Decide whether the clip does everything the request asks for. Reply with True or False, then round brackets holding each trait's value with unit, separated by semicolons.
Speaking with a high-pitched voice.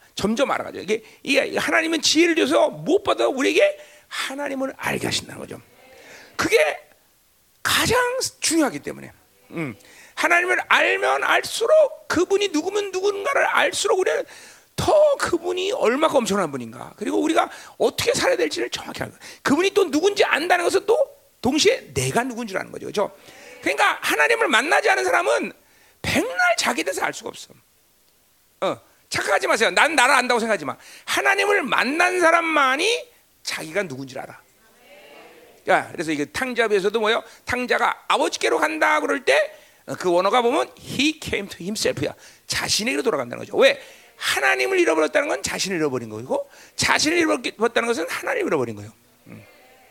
True (300 Hz)